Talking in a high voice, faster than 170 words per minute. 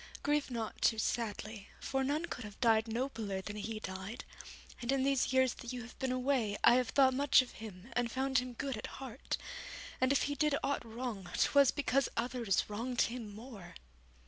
Yes: high, 245 Hz; average, 195 wpm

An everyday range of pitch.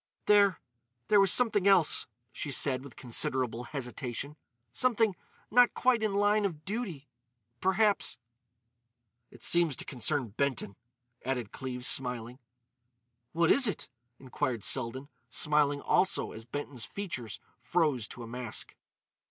No: wide, 7.9 semitones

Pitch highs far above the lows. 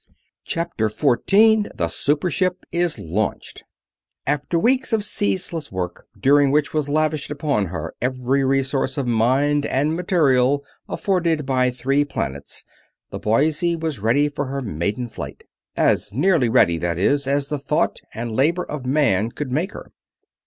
No: average, 4.4 semitones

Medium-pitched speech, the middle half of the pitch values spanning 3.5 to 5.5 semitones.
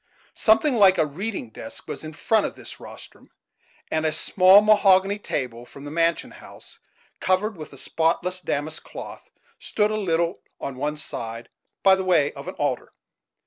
Yes: medium, 170 Hz; average, 4.8 semitones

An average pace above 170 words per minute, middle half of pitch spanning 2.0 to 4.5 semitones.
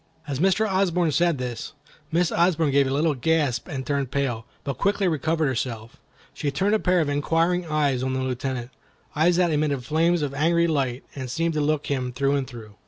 Yes: average, 195 wpm; average, 4.2 semitones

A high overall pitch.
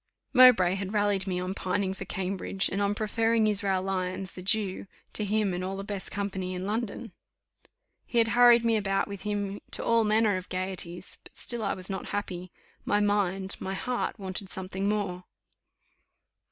Yes: high, 195 Hz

